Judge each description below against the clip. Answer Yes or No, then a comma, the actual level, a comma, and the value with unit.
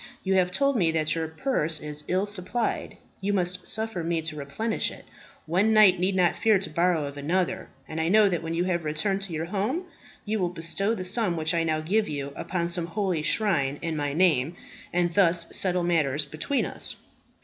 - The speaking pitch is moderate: Yes, medium, 175 Hz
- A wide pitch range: No, average, 3.6 semitones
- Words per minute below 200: No, fast, 205 wpm